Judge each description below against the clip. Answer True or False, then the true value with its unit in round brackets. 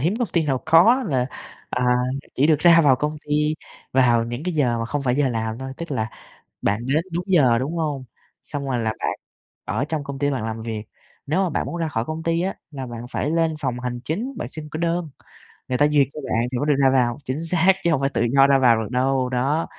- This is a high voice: False (140 Hz)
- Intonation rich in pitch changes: False (4.3 semitones)